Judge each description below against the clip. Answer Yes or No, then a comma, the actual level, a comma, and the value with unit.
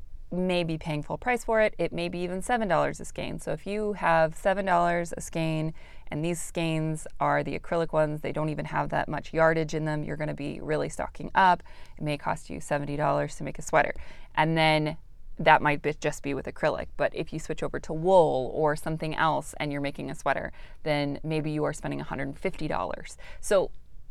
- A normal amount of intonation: No, narrow, 2.3 semitones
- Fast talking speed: Yes, fast, 225 wpm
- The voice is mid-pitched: Yes, medium, 155 Hz